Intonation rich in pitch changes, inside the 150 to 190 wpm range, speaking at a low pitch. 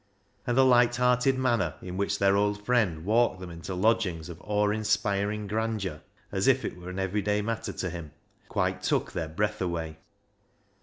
No: average, 3.7 semitones; average, 175 wpm; low, 105 Hz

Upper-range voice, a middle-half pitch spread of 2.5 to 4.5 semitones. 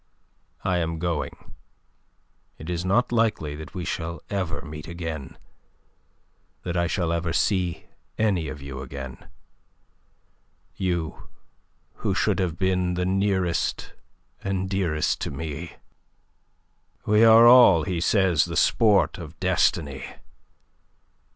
No: very low, 85 Hz; average, 3.0 semitones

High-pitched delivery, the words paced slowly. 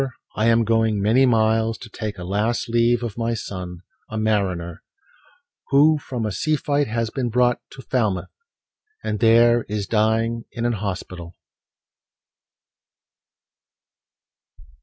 No: low, 115 Hz; slow, 130 wpm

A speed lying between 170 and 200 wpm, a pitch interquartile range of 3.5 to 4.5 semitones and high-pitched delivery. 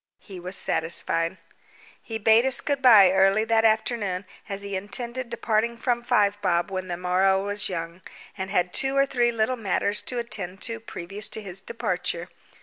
Yes: average, 175 wpm; average, 3.8 semitones; high, 205 Hz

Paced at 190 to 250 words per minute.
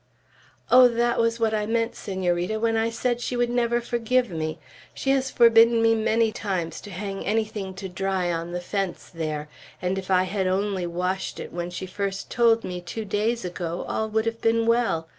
Yes: average, 200 wpm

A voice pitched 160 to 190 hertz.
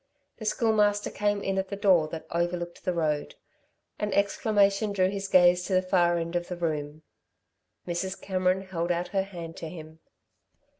Yes: medium, 185 Hz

